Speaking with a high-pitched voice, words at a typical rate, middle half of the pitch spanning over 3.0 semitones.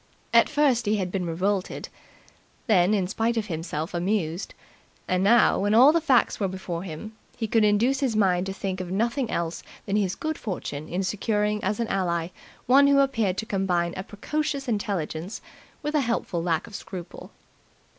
Yes: high, 200 Hz; average, 180 wpm; average, 4.2 semitones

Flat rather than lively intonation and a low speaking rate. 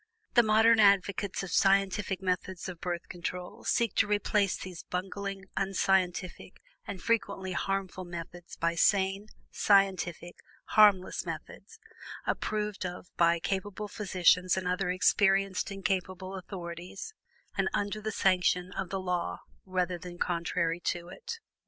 Yes: narrow, 1.8 semitones; slow, 130 wpm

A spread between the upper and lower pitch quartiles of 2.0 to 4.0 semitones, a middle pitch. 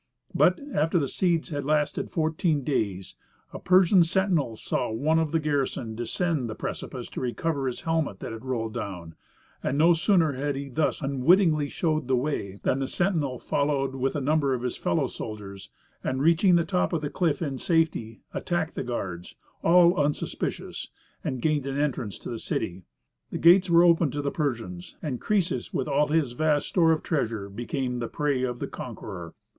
No: average, 4.7 semitones; medium, 145 Hz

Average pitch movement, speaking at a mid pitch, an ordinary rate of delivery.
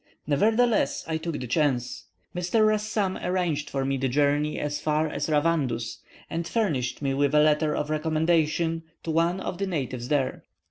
Yes: average, 3.3 semitones; medium, 155 Hz; average, 170 wpm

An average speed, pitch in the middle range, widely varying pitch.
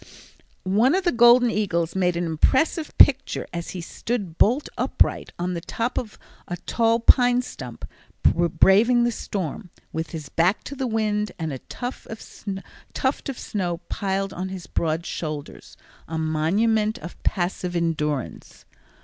No: average, 145 wpm; high, 195 Hz; wide, 5.7 semitones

